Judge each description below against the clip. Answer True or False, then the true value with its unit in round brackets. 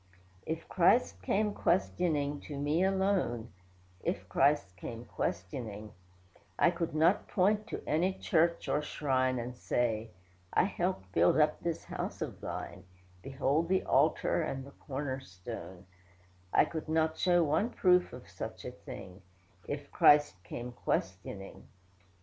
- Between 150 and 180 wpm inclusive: False (140 wpm)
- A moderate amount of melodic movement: False (6.7 semitones)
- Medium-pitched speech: True (145 Hz)